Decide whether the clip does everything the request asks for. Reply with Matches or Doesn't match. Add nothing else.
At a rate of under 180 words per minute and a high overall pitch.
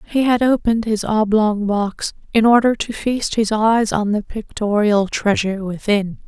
Matches